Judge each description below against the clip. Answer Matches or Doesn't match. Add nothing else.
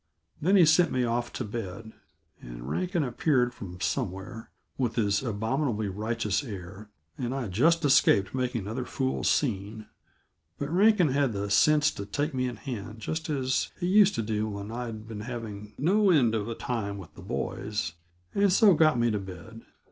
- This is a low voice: Matches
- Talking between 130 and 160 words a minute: Doesn't match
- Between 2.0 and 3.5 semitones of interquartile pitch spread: Doesn't match